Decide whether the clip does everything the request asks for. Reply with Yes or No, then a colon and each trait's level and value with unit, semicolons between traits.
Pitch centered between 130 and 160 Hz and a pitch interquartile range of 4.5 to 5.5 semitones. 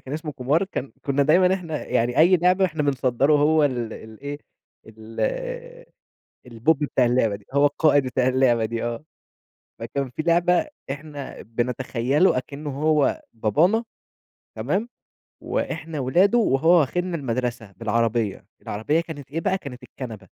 Yes: medium, 140 Hz; average, 5.2 semitones